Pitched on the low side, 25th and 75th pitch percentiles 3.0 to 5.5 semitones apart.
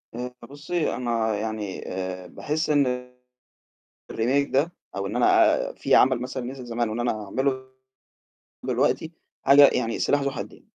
Yes: low, 125 Hz; average, 3.7 semitones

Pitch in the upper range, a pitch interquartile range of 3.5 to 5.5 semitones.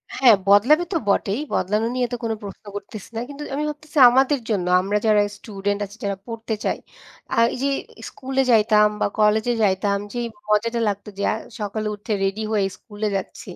No: high, 215 Hz; average, 2.9 semitones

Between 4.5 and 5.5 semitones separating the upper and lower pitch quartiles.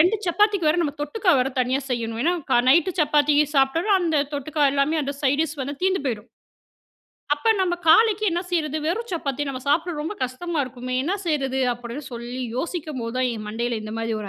Yes: average, 5.2 semitones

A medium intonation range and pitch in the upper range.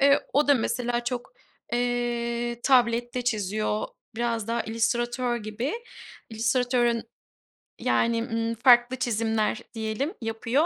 No: narrow, 1.4 semitones; high, 235 Hz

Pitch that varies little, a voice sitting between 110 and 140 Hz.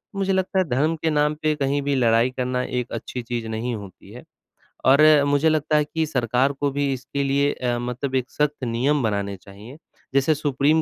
No: average, 3.3 semitones; low, 135 Hz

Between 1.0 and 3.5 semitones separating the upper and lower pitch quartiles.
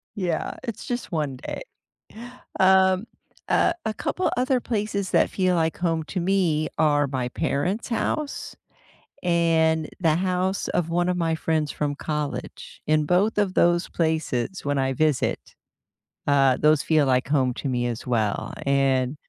No: average, 4.6 semitones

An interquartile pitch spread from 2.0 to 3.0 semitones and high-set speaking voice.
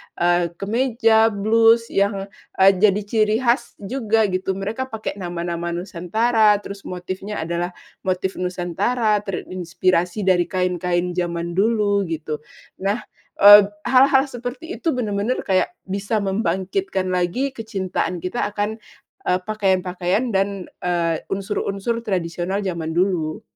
No: average, 3.6 semitones; high, 195 Hz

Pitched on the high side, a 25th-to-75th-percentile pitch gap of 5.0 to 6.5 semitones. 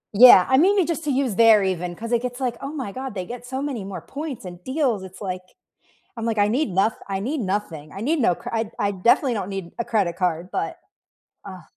Yes: high, 220 Hz; wide, 5.4 semitones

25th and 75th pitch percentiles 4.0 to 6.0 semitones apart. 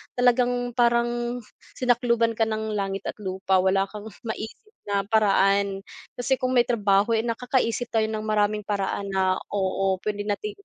No: average, 3.3 semitones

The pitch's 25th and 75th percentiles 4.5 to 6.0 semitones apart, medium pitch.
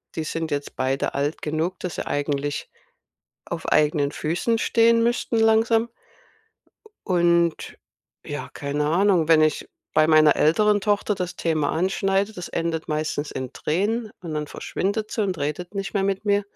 Yes: average, 5.0 semitones; medium, 170 Hz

